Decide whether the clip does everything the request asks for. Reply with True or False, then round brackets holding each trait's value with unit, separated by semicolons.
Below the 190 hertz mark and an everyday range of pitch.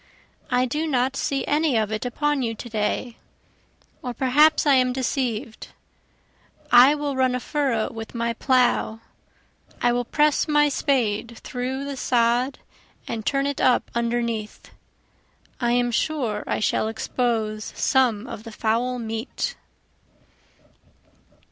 False (245 Hz; 3.0 semitones)